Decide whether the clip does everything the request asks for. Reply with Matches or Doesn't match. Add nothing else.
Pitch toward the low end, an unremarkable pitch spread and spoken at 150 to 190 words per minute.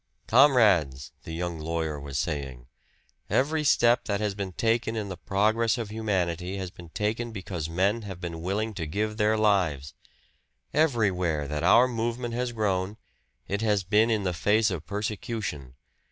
Matches